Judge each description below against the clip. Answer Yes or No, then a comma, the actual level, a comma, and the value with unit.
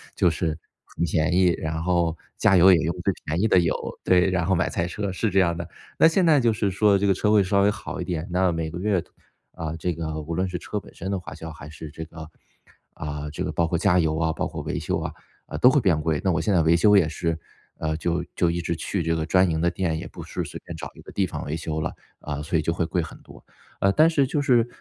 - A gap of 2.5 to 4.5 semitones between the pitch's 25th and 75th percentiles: Yes, average, 3.1 semitones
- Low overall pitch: Yes, very low, 85 Hz